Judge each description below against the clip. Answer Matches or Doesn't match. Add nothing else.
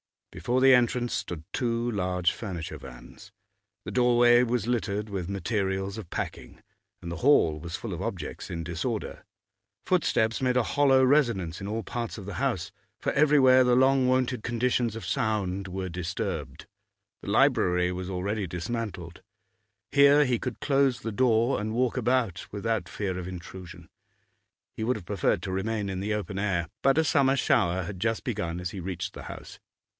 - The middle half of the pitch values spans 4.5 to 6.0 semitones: Matches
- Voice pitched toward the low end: Matches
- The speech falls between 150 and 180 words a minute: Matches